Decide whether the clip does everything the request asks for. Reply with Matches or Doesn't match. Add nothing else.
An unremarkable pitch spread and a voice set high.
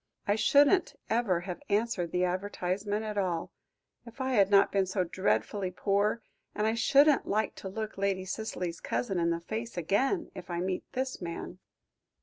Matches